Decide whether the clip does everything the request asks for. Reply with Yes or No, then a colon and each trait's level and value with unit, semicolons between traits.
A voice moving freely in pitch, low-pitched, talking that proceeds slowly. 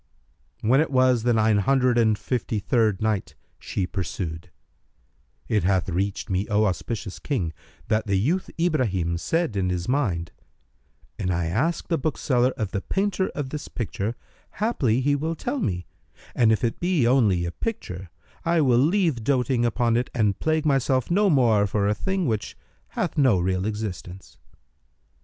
No: wide, 6.2 semitones; low, 115 Hz; average, 165 wpm